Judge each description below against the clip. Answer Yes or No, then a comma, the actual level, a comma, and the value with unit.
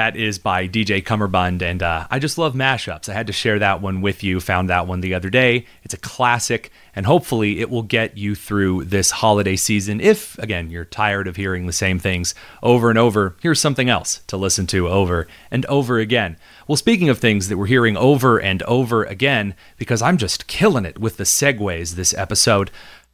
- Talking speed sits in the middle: No, fast, 210 wpm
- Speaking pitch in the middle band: No, low, 105 Hz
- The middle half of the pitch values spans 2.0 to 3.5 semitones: No, average, 4.2 semitones